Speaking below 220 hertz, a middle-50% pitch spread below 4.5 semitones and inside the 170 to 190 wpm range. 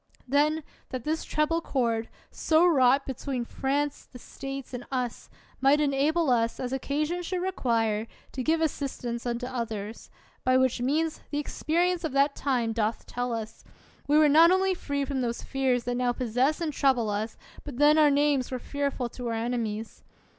No: very high, 270 Hz; average, 3.7 semitones; average, 175 wpm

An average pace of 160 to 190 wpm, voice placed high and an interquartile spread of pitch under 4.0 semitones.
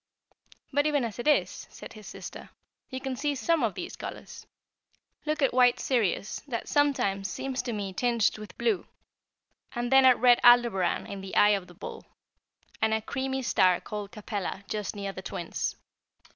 No: average, 175 wpm; high, 235 Hz; average, 4.8 semitones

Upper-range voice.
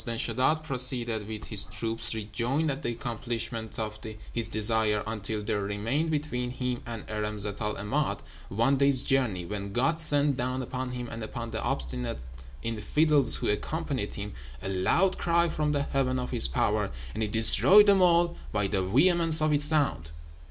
No: low, 120 Hz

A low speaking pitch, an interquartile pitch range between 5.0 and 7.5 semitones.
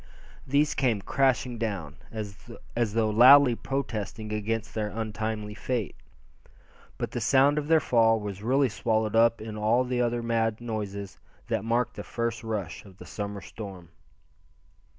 No: low, 115 Hz; narrow, 2.6 semitones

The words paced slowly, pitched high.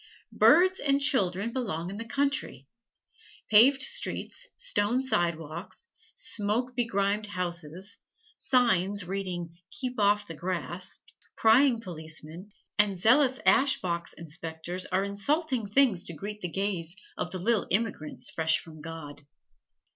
Yes: slow, 125 wpm; high, 200 Hz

